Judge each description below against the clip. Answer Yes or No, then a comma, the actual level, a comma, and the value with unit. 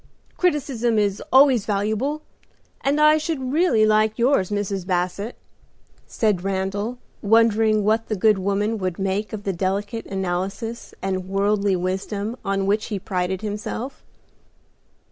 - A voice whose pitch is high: Yes, high, 210 Hz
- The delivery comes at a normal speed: No, slow, 130 wpm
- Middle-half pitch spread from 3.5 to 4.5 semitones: No, average, 2.9 semitones